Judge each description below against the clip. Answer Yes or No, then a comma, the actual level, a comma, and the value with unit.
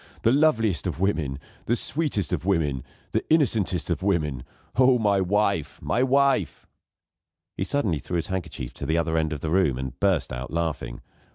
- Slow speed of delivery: No, average, 175 wpm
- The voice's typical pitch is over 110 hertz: No, very low, 90 Hz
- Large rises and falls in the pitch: Yes, wide, 6.4 semitones